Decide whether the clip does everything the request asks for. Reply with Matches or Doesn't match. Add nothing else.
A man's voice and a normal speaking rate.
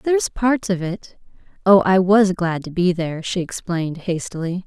Doesn't match